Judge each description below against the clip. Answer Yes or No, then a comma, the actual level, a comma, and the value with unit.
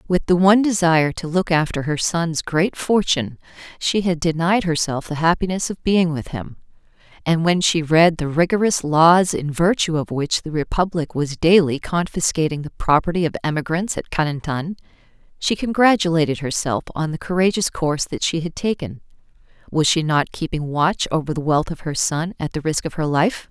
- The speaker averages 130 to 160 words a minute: No, average, 180 wpm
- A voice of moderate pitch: Yes, medium, 165 Hz